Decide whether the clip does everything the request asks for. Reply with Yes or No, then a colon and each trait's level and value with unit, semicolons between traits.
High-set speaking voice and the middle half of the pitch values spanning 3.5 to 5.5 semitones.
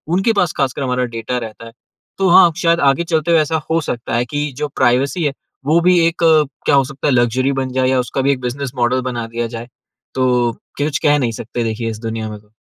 No: low, 130 Hz; average, 3.9 semitones